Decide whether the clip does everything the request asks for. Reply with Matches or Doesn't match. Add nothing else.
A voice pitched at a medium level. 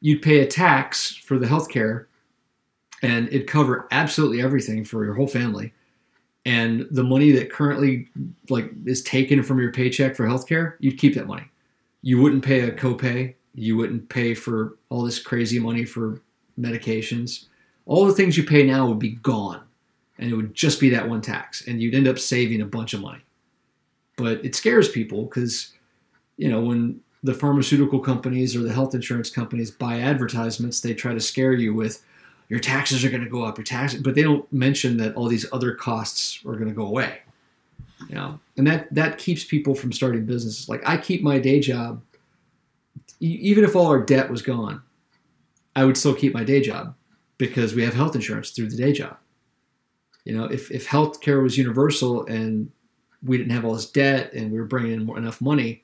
Doesn't match